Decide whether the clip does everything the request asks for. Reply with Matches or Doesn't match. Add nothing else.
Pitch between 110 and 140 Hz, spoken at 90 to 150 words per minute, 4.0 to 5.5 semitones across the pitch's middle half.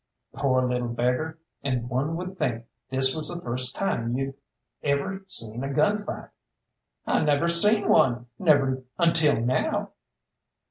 Matches